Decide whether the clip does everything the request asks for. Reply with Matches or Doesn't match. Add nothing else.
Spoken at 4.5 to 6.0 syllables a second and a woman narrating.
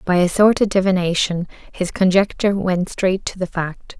Matches